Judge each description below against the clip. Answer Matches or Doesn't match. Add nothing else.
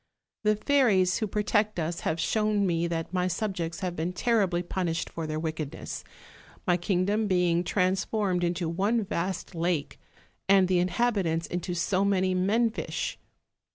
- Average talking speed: Matches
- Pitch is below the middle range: Doesn't match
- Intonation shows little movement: Doesn't match